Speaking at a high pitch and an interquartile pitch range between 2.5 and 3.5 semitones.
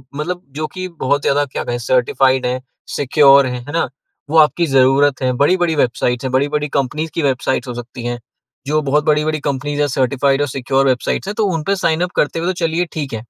No: medium, 145 Hz; average, 3.1 semitones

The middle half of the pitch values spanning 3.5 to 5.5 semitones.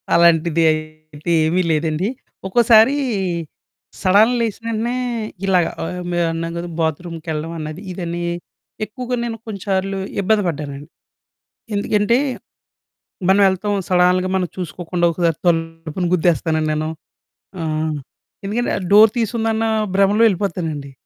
Yes: average, 4.1 semitones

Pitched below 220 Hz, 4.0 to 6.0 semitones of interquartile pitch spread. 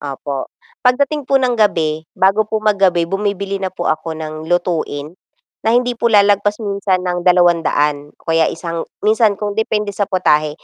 Yes: high, 190 Hz; average, 4.3 semitones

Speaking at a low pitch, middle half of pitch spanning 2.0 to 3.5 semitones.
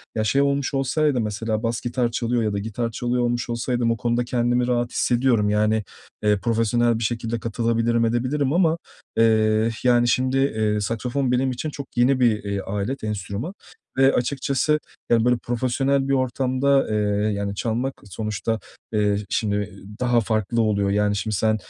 Yes: low, 120 Hz; average, 2.8 semitones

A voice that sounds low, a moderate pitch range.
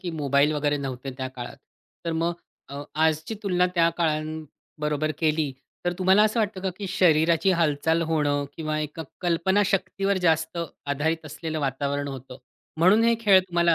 No: medium, 160 Hz; average, 3.5 semitones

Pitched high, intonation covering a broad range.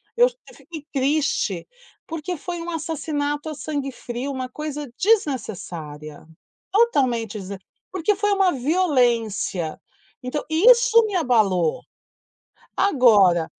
Yes: very high, 290 Hz; wide, 7.0 semitones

